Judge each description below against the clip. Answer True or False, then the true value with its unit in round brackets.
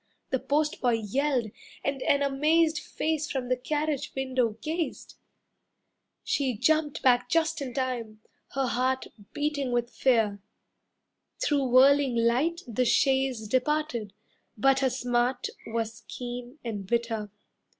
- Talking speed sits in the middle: False (120 wpm)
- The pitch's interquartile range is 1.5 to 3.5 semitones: True (3.1 semitones)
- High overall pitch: True (260 Hz)